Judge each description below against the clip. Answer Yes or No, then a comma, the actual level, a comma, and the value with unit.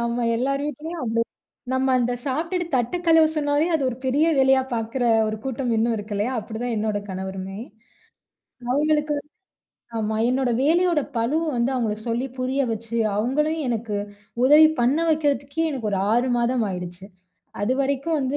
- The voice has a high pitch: Yes, very high, 255 Hz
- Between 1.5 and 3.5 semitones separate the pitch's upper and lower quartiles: No, average, 4.4 semitones